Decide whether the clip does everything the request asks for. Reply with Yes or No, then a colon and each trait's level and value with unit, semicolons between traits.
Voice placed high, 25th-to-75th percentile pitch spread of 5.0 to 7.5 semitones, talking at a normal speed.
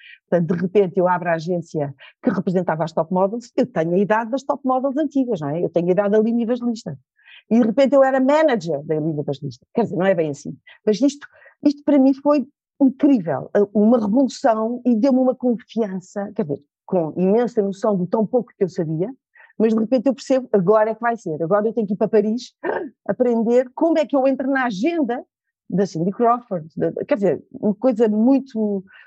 No: high, 225 Hz; wide, 5.6 semitones; fast, 210 wpm